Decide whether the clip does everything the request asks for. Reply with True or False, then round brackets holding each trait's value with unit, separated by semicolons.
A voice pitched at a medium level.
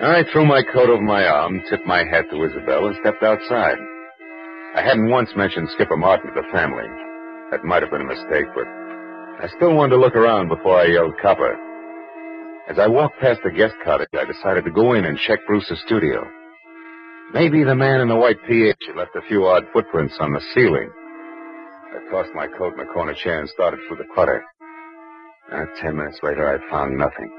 True (170 Hz)